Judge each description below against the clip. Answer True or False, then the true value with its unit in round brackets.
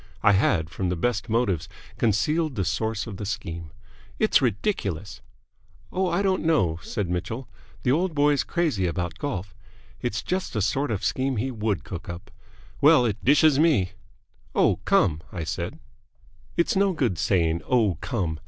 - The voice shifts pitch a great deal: True (7.9 semitones)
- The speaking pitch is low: True (110 Hz)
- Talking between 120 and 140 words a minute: False (160 wpm)